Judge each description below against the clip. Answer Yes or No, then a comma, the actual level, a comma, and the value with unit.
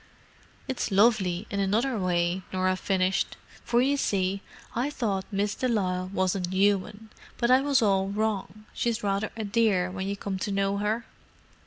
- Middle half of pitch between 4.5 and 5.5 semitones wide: No, average, 2.8 semitones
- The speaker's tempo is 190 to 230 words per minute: No, average, 165 wpm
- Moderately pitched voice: No, high, 200 Hz